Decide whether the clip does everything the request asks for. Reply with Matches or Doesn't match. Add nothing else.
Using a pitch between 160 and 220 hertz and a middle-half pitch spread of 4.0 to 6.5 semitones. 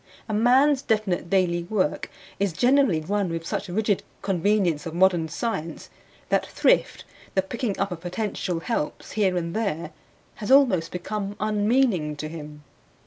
Matches